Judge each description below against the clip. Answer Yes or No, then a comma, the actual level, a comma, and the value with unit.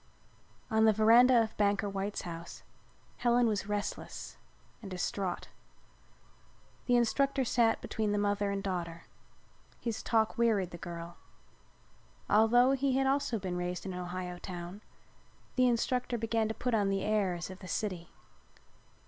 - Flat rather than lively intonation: No, average, 4.1 semitones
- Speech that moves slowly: No, average, 145 wpm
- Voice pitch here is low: No, high, 205 Hz